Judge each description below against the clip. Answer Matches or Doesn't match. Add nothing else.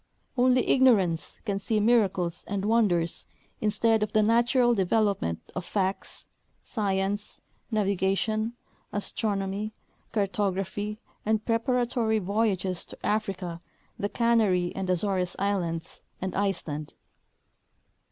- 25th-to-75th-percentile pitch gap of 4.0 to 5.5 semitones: Doesn't match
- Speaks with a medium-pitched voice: Doesn't match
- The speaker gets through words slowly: Matches